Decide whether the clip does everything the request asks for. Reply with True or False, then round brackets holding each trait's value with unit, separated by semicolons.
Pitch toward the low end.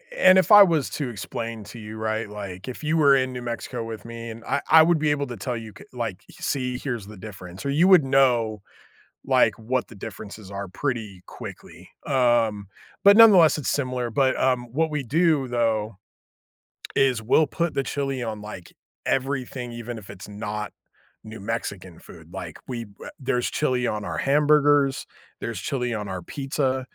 True (120 Hz)